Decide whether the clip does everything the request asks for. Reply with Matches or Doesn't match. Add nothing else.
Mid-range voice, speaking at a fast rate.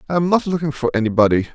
Matches